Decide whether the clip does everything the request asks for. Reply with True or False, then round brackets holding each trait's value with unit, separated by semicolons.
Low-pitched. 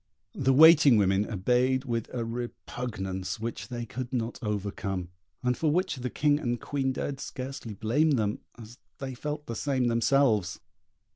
True (125 Hz)